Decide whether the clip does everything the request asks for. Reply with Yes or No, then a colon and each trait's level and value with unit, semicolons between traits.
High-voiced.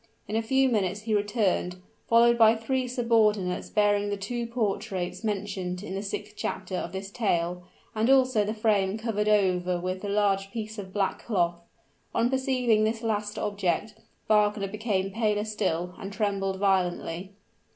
Yes: high, 205 Hz